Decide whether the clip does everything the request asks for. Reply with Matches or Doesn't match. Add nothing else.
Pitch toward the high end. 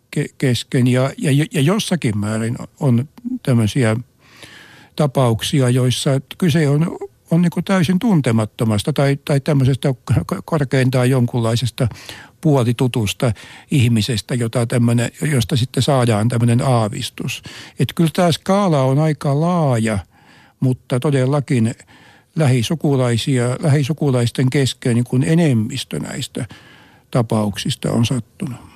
Doesn't match